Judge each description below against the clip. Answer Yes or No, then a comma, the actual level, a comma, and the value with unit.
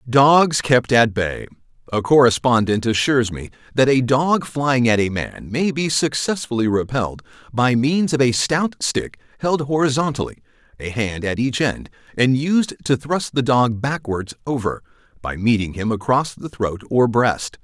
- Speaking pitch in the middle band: No, low, 125 Hz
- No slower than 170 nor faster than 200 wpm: No, average, 160 wpm